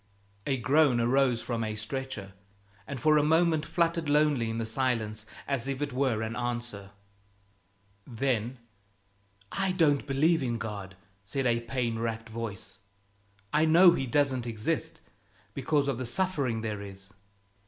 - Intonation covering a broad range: No, average, 4.4 semitones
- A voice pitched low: Yes, low, 125 Hz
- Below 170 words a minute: Yes, average, 145 wpm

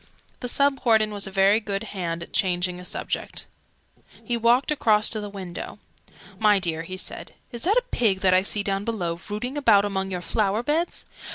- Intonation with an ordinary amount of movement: Yes, average, 3.8 semitones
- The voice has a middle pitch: No, high, 205 Hz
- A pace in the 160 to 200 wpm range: Yes, average, 195 wpm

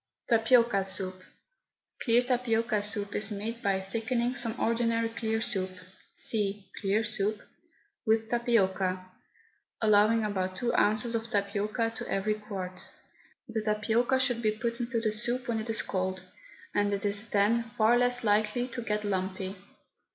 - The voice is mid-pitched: No, high, 220 Hz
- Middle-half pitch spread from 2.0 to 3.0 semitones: Yes, narrow, 2.4 semitones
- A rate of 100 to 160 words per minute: Yes, average, 145 wpm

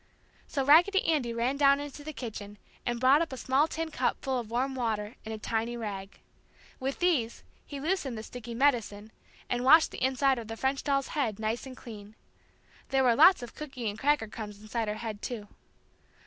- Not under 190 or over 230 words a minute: Yes, average, 200 wpm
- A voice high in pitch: Yes, high, 245 Hz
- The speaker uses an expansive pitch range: No, average, 4.0 semitones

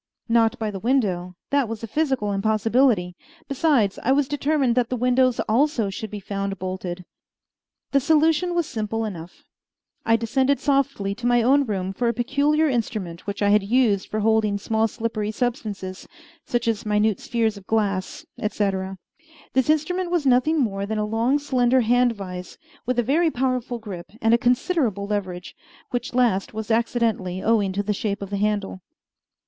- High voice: Yes, high, 225 Hz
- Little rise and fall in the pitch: No, average, 4.1 semitones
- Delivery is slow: No, average, 170 wpm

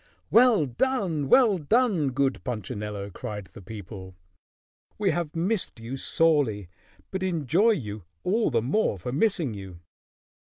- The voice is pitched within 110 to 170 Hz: Yes, medium, 140 Hz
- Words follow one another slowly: Yes, slow, 130 wpm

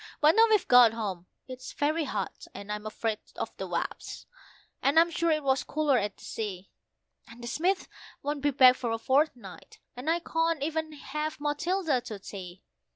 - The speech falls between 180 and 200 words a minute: Yes, average, 185 wpm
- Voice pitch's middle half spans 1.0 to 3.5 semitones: No, wide, 5.6 semitones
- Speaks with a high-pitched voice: Yes, very high, 275 Hz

